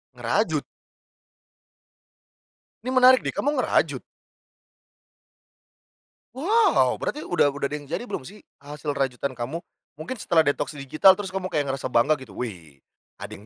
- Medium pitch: Yes, medium, 150 Hz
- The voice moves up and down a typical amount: No, wide, 6.2 semitones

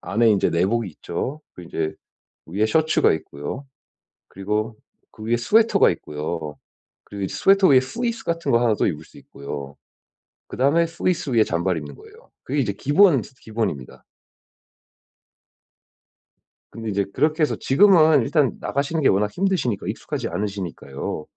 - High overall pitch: No, low, 115 Hz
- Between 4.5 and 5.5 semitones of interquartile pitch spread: No, wide, 8.7 semitones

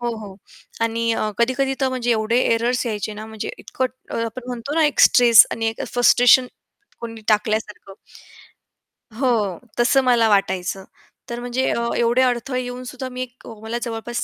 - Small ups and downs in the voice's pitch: Yes, narrow, 2.2 semitones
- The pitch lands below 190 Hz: No, high, 235 Hz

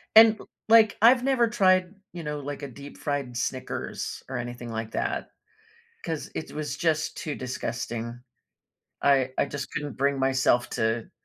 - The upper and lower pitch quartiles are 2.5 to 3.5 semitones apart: No, wide, 5.4 semitones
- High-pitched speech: No, medium, 140 Hz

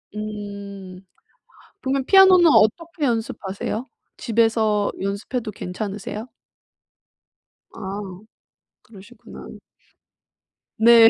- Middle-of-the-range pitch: No, high, 215 Hz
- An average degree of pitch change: Yes, average, 3.2 semitones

